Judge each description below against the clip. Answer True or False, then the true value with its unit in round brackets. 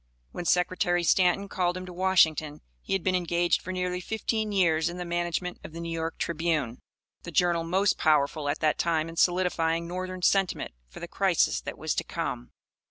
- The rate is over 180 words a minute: True (190 wpm)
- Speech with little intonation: True (2.0 semitones)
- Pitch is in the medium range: True (175 Hz)